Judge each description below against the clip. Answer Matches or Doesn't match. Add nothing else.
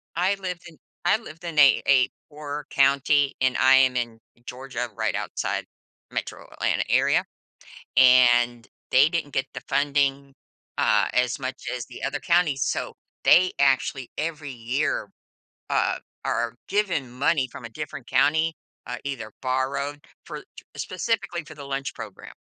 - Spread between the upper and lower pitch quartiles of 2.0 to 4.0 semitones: Matches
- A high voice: Doesn't match